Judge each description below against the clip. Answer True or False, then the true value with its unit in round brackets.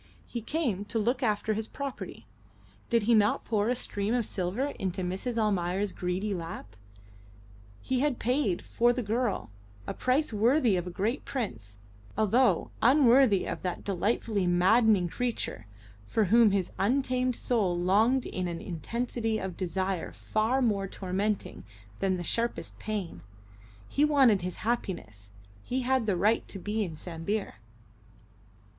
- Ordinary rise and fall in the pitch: True (4.6 semitones)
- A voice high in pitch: True (210 Hz)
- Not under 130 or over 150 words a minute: True (145 wpm)